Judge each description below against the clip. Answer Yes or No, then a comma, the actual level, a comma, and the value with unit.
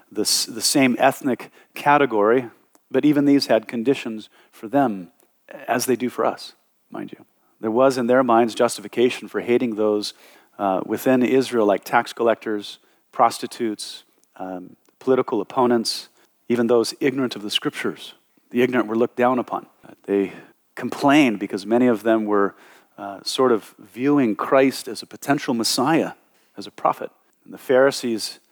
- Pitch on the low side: Yes, low, 120 Hz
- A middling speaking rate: Yes, average, 155 wpm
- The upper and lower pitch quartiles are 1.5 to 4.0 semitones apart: Yes, average, 3.3 semitones